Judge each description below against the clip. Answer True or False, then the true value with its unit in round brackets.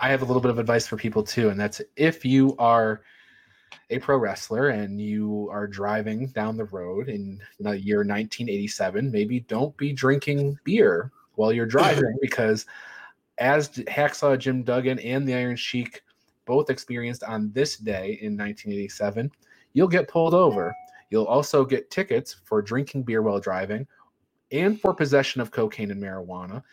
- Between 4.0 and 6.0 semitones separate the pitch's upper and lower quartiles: True (4.4 semitones)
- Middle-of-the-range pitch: False (120 Hz)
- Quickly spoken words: False (165 wpm)